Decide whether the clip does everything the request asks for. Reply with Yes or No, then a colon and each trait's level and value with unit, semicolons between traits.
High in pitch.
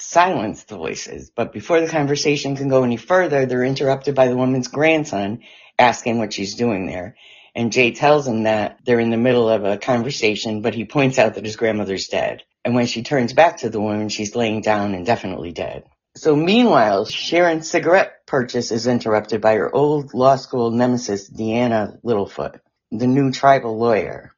No: low, 120 Hz